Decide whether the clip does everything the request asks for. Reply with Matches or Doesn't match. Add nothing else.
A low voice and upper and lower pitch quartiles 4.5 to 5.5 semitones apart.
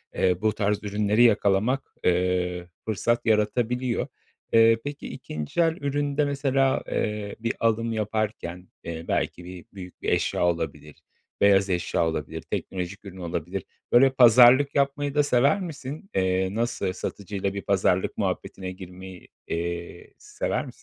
Matches